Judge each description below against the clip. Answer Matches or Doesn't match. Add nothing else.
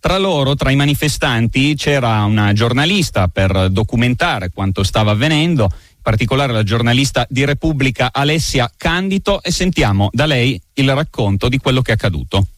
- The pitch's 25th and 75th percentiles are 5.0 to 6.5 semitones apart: Matches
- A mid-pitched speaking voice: Doesn't match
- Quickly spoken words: Doesn't match